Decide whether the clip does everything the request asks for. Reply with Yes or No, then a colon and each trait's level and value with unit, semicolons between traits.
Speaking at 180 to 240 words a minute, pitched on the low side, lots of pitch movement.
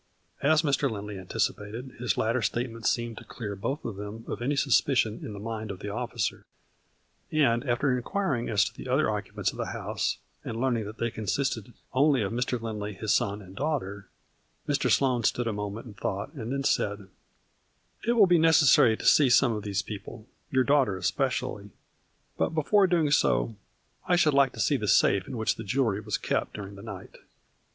No: average, 200 wpm; low, 115 Hz; average, 4.8 semitones